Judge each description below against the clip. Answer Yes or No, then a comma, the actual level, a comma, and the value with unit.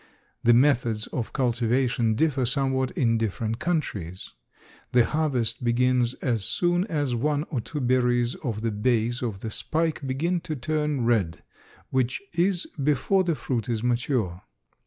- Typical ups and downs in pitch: Yes, average, 4.2 semitones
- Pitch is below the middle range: Yes, low, 125 Hz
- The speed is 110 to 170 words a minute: Yes, average, 145 wpm